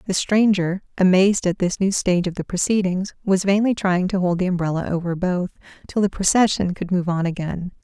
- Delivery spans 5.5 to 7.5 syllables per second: Yes, 5.6 syllables/s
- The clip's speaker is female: Yes, female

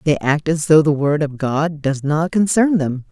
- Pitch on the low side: No, medium, 155 Hz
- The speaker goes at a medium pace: No, fast, 230 wpm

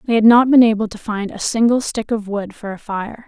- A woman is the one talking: Yes, female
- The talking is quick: Yes, fast, 275 wpm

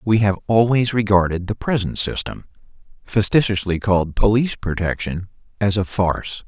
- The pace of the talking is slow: Yes, slow, 110 wpm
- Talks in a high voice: No, low, 100 Hz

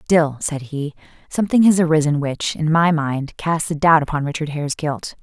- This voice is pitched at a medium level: Yes, medium, 155 Hz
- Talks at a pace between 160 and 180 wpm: No, average, 195 wpm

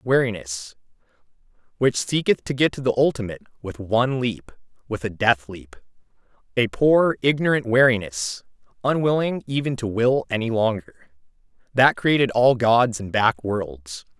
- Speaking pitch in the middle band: No, low, 115 Hz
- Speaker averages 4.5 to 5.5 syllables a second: Yes, 4.6 syllables/s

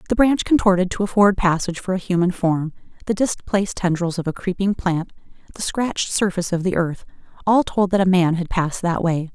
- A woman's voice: Yes, female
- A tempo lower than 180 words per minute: No, average, 195 wpm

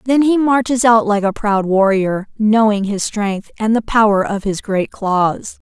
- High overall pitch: Yes, high, 215 Hz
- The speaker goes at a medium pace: Yes, average, 190 wpm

